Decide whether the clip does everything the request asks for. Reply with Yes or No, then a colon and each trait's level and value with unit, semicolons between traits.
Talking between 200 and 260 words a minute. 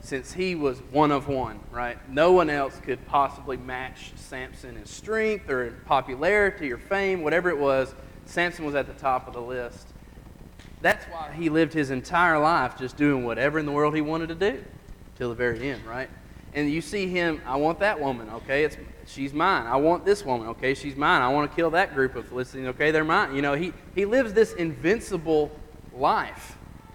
Yes: fast, 205 wpm